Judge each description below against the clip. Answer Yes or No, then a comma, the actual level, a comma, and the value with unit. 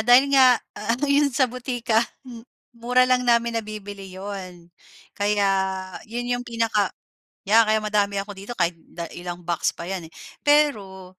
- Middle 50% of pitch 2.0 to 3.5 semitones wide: No, average, 3.9 semitones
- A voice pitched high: Yes, high, 220 Hz